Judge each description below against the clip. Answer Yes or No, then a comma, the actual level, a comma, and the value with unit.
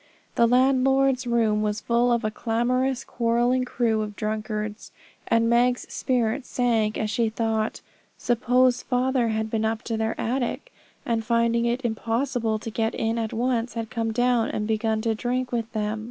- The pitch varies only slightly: Yes, narrow, 2.0 semitones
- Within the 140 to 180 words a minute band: Yes, average, 170 wpm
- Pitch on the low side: No, high, 230 Hz